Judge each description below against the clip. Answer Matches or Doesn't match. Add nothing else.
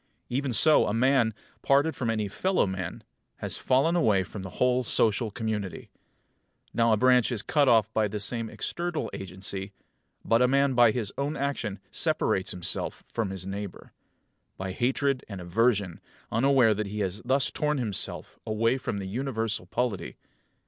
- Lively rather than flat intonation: Doesn't match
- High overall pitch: Doesn't match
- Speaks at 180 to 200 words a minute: Doesn't match